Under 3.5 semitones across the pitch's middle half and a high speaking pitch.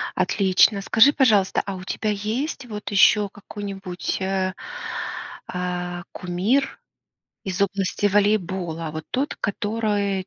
Yes: narrow, 2.4 semitones; high, 195 Hz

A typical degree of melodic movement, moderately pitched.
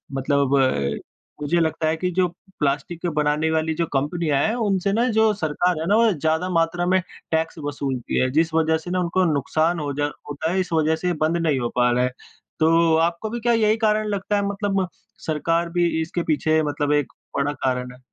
Yes: average, 3.6 semitones; medium, 160 Hz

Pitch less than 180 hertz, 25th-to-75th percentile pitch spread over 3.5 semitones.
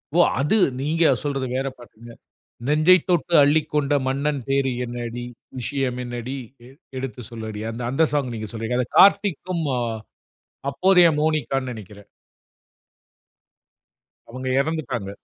Yes: low, 135 Hz; average, 4.1 semitones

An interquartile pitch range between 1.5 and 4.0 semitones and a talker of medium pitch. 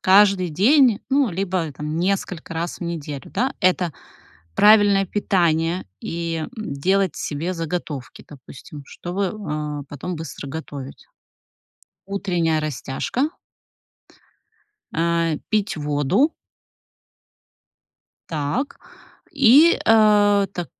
No: average, 4.9 semitones; medium, 175 Hz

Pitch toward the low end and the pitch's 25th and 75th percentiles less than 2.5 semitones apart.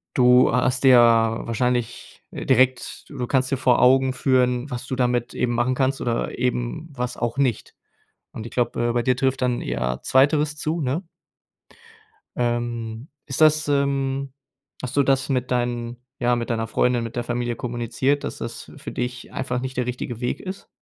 Yes: low, 125 Hz; narrow, 1.8 semitones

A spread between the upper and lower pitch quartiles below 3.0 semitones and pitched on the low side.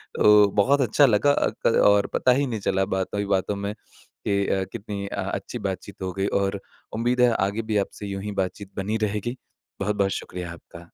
Yes: narrow, 2.4 semitones; low, 100 Hz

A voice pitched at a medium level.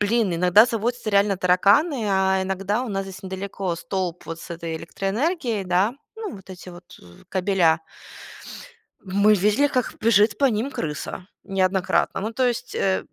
No: high, 195 Hz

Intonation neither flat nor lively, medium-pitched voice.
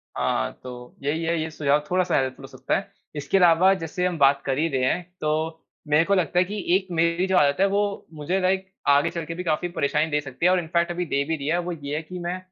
Yes: average, 3.5 semitones; medium, 165 Hz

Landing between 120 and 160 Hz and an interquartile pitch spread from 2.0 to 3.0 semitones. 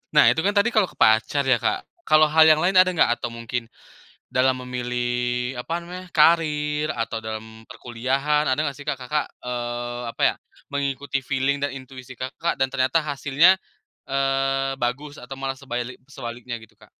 No: low, 135 Hz; average, 3.4 semitones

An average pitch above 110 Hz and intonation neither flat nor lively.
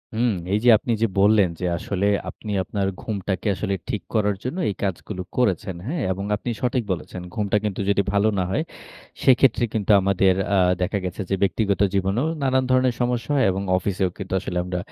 No: low, 100 Hz; average, 3.7 semitones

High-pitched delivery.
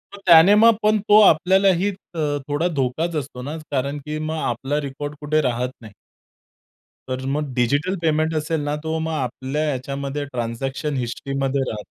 No: medium, 145 Hz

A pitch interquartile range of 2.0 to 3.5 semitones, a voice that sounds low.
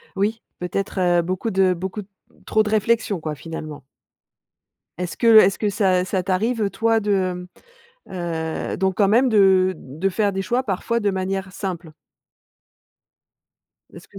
No: average, 2.8 semitones; high, 190 Hz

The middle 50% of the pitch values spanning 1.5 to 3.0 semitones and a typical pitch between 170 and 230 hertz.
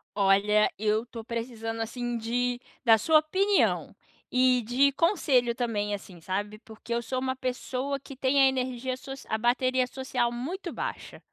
No: average, 2.7 semitones; high, 245 Hz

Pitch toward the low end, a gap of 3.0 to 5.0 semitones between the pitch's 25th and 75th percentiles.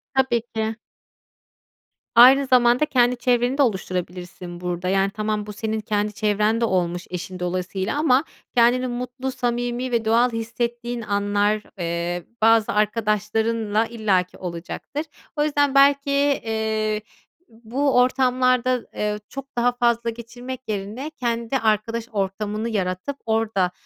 No: high, 225 Hz; average, 3.3 semitones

